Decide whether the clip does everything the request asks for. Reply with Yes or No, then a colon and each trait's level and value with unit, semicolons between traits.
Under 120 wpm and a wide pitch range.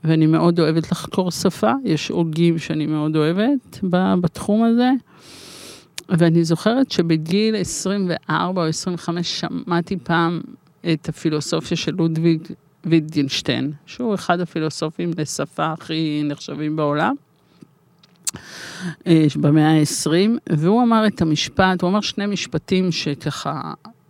No: average, 105 wpm; average, 3.0 semitones